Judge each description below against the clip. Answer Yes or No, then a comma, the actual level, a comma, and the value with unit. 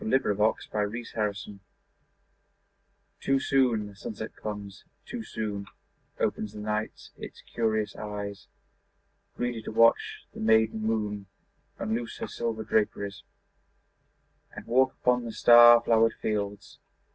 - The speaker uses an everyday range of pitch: No, narrow, 2.0 semitones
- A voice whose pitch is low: Yes, low, 110 Hz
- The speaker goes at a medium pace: No, slow, 120 wpm